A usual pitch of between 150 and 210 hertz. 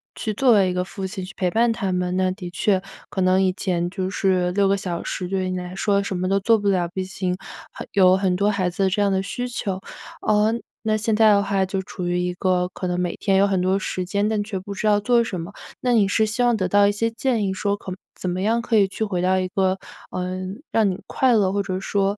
Yes: high, 195 Hz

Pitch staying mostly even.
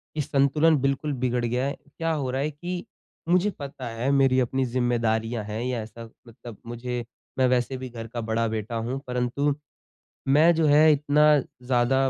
No: average, 3.2 semitones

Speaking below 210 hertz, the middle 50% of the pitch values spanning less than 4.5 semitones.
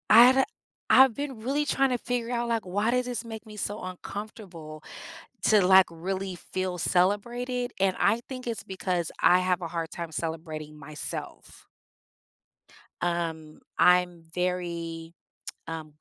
No: medium, 185 Hz; wide, 5.6 semitones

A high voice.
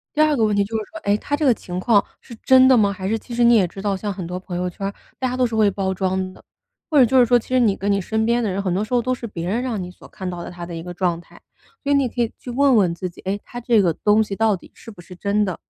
Yes: high, 205 Hz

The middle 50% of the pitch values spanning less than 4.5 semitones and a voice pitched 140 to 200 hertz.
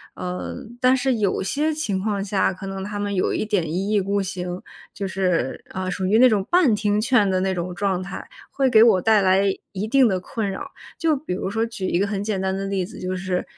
Yes: average, 2.7 semitones; high, 195 Hz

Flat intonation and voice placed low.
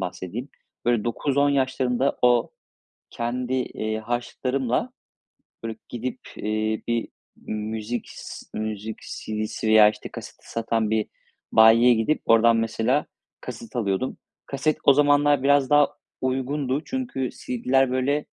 No: average, 3.3 semitones; low, 120 Hz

